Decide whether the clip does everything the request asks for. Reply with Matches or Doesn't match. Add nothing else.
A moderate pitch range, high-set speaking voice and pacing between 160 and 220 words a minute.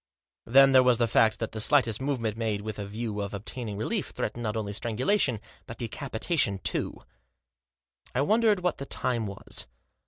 Doesn't match